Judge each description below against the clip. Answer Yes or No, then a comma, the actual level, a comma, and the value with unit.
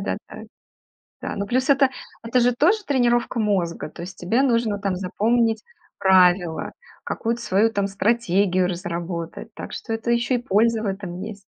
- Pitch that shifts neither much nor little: Yes, average, 4.1 semitones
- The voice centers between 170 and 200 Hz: No, high, 210 Hz